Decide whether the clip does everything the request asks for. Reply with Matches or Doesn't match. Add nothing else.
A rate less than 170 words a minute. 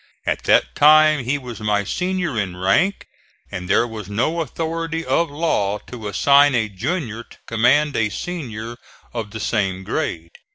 Matches